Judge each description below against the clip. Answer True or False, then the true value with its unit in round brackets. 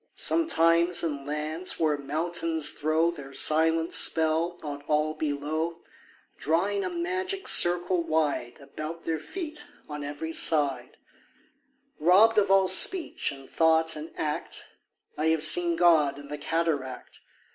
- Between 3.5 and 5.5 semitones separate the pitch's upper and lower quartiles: False (2.7 semitones)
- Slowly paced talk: True (130 wpm)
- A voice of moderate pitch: True (160 Hz)